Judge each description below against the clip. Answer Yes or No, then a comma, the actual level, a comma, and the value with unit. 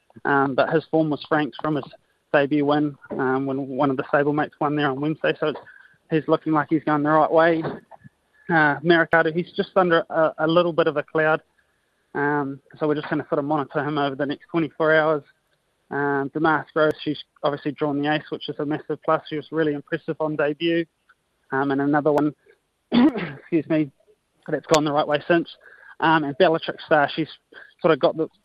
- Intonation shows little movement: Yes, narrow, 1.6 semitones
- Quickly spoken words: Yes, fast, 210 wpm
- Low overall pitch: No, medium, 155 Hz